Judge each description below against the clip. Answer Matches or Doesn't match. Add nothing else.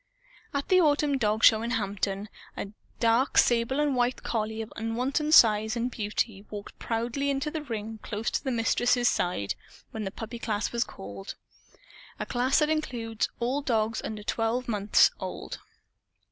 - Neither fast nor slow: Matches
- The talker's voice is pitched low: Doesn't match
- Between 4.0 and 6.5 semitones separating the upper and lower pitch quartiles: Doesn't match